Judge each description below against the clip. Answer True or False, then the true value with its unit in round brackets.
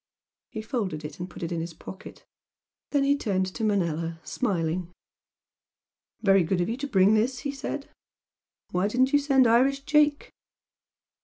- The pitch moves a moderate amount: False (7.3 semitones)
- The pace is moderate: True (160 wpm)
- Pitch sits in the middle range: False (215 Hz)